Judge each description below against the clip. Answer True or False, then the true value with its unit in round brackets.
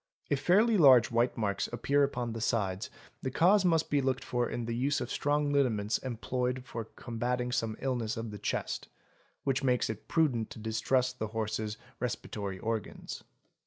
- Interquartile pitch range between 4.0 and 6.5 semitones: False (3.4 semitones)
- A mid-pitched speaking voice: False (125 Hz)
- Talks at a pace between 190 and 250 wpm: False (170 wpm)